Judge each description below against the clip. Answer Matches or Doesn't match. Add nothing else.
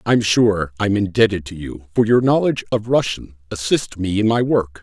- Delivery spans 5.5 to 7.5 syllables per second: Doesn't match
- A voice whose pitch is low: Matches